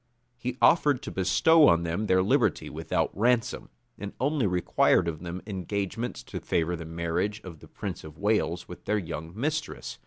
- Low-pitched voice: Yes, very low, 95 Hz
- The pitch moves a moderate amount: No, wide, 5.7 semitones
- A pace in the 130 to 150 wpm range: No, average, 175 wpm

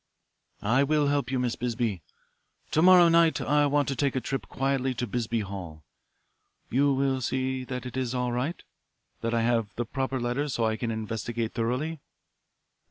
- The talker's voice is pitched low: Yes, low, 125 Hz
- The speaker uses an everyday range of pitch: Yes, average, 3.1 semitones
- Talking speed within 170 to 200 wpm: Yes, average, 175 wpm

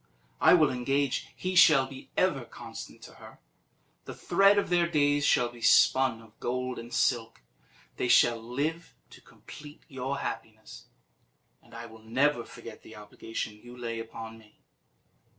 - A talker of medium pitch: No, low, 125 Hz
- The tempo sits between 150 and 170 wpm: Yes, average, 155 wpm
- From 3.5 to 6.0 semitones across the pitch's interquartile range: Yes, average, 4.1 semitones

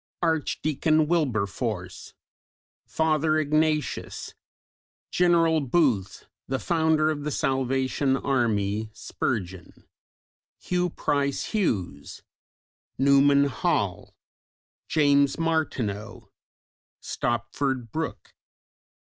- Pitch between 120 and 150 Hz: Yes, medium, 140 Hz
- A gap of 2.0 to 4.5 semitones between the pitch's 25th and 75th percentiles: No, average, 4.9 semitones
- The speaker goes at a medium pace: No, slow, 70 wpm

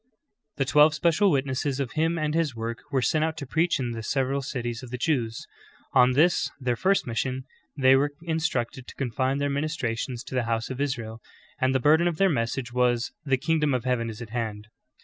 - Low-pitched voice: Yes, low, 130 Hz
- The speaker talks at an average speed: No, fast, 215 wpm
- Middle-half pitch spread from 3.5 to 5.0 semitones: Yes, average, 3.9 semitones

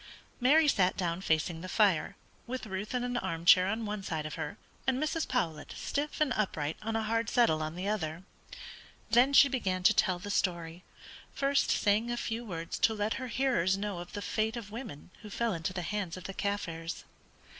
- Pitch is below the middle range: No, high, 205 Hz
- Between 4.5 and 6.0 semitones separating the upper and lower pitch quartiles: Yes, average, 5.1 semitones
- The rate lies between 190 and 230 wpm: Yes, fast, 205 wpm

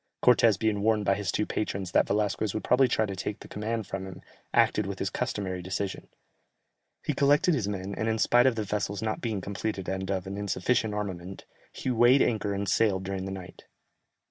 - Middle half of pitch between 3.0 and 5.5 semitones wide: No, narrow, 2.5 semitones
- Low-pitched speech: Yes, low, 105 Hz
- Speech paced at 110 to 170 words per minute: No, fast, 205 wpm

